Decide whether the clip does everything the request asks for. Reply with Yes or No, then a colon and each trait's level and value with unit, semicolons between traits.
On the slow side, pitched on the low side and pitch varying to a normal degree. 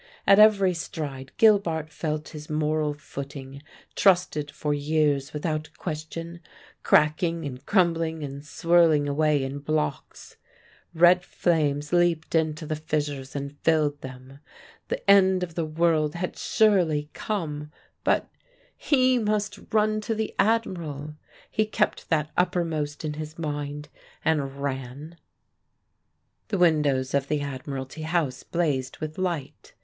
No: slow, 125 wpm; medium, 155 Hz; average, 3.1 semitones